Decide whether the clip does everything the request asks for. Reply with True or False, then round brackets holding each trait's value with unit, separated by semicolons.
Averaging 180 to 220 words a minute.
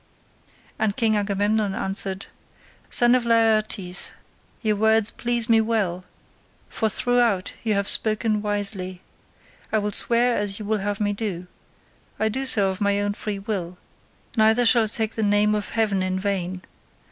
False (160 wpm)